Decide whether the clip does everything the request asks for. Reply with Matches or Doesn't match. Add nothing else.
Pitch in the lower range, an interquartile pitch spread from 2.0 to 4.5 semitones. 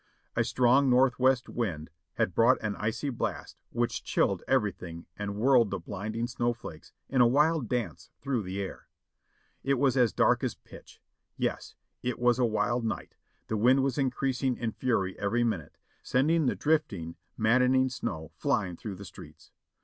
Matches